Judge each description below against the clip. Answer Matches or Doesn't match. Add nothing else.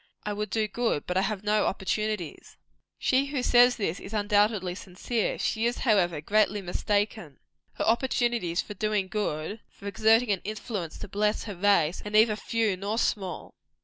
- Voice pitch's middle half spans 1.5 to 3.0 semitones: Matches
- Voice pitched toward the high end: Matches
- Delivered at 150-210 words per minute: Matches